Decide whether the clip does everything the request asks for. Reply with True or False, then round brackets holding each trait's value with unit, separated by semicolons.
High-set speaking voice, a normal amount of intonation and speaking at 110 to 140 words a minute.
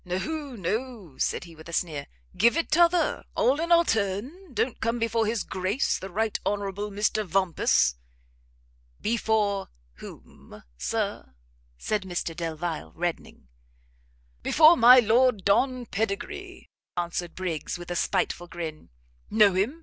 False (205 Hz; 5.8 semitones; 135 wpm)